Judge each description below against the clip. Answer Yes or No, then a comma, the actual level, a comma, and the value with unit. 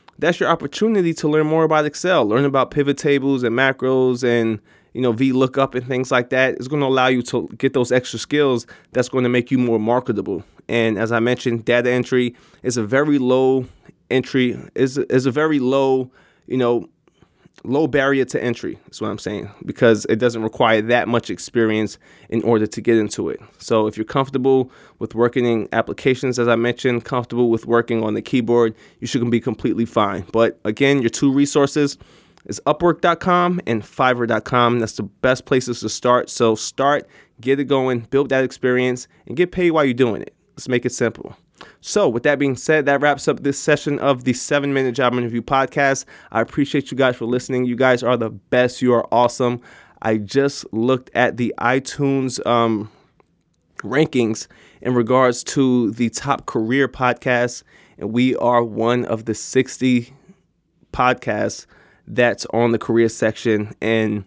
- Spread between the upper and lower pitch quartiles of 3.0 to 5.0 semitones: No, narrow, 2.5 semitones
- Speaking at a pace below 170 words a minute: No, average, 180 wpm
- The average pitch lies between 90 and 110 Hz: No, low, 125 Hz